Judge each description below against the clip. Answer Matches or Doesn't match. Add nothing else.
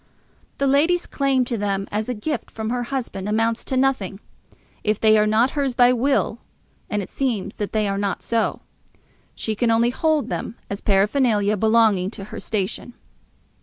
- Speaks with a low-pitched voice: Doesn't match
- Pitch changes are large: Doesn't match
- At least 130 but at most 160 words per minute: Doesn't match